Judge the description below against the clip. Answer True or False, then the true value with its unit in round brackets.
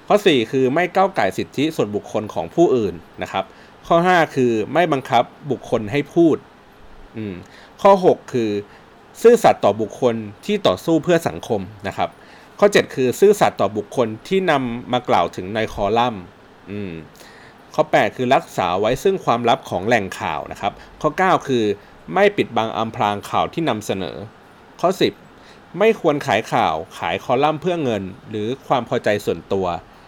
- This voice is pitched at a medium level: False (125 Hz)